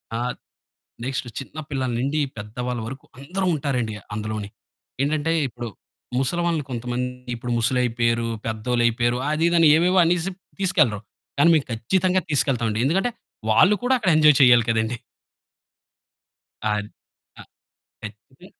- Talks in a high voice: No, low, 125 Hz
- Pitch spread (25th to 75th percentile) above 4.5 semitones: Yes, wide, 5.6 semitones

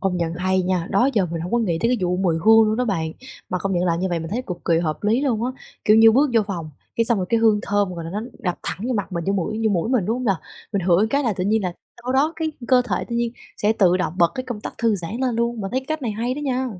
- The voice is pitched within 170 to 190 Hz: No, high, 210 Hz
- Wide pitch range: No, average, 4.8 semitones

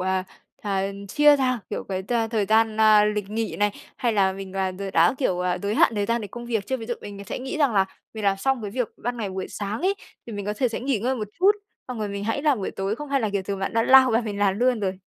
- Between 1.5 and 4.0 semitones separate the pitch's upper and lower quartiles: Yes, average, 3.6 semitones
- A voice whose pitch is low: No, high, 215 Hz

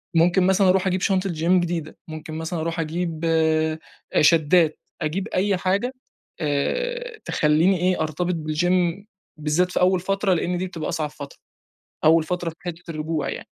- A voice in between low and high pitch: Yes, medium, 170 Hz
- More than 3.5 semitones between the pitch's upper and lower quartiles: No, average, 2.7 semitones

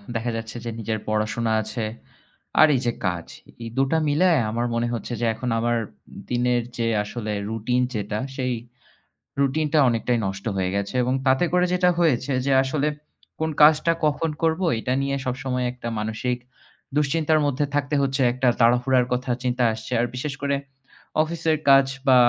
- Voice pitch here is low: Yes, low, 125 Hz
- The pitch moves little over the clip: No, average, 3.7 semitones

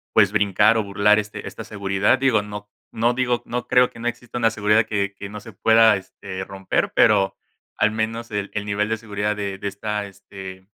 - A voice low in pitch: Yes, low, 105 Hz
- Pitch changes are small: Yes, narrow, 2.0 semitones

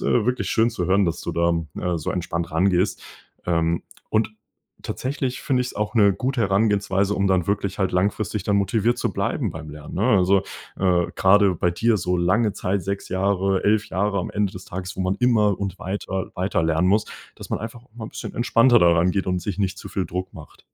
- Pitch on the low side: Yes, very low, 95 Hz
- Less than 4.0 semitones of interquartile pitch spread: Yes, average, 2.7 semitones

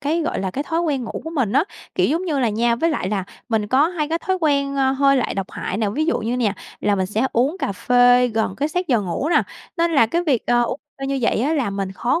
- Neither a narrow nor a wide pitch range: No, wide, 5.7 semitones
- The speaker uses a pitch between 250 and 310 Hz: Yes, very high, 265 Hz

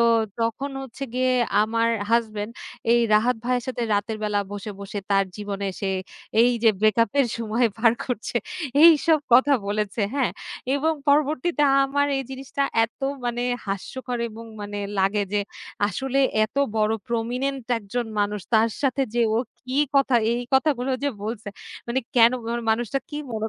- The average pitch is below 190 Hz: No, high, 235 Hz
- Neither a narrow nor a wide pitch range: Yes, average, 3.7 semitones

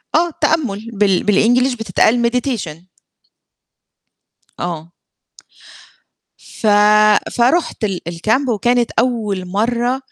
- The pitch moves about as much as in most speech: Yes, average, 4.0 semitones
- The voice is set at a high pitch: Yes, high, 225 Hz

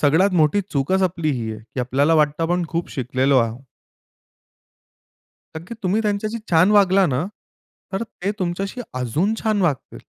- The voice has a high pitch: No, medium, 170 Hz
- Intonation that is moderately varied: No, wide, 6.0 semitones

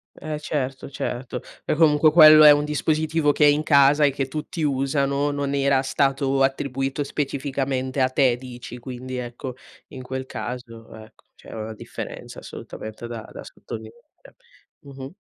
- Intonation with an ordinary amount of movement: No, narrow, 2.3 semitones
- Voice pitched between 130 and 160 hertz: Yes, low, 135 Hz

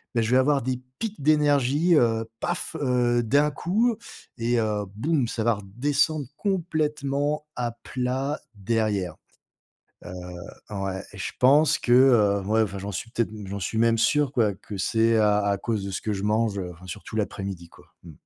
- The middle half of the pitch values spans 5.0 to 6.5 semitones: Yes, wide, 5.6 semitones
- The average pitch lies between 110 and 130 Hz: Yes, low, 115 Hz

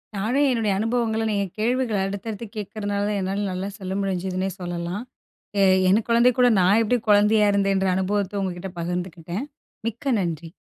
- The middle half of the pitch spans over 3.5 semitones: No, average, 3.0 semitones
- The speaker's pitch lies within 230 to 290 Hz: No, high, 200 Hz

